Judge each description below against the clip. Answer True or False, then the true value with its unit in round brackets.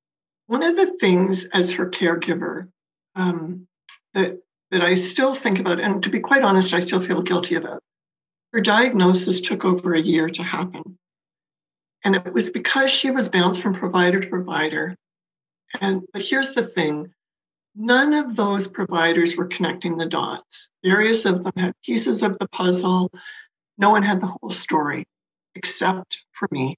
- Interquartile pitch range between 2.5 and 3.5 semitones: True (2.8 semitones)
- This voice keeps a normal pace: True (165 wpm)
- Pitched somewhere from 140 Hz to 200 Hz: True (185 Hz)